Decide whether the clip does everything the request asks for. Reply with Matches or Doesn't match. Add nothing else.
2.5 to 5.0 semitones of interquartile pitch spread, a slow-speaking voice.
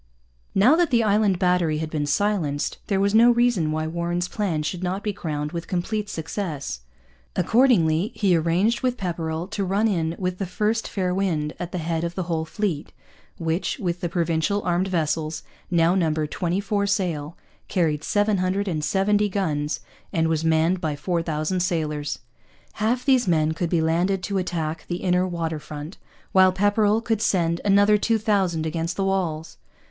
Doesn't match